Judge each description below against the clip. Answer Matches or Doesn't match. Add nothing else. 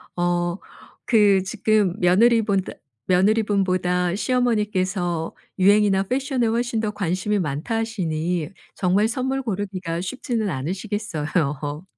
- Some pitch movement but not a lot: Matches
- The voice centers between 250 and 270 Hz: Doesn't match